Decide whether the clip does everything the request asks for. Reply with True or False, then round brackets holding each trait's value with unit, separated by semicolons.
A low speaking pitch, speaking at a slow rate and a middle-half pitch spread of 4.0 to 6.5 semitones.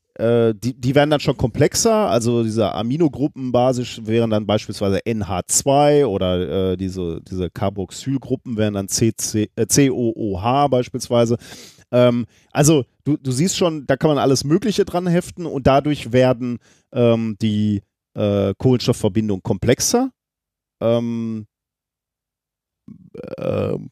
True (120 Hz; 120 wpm; 4.4 semitones)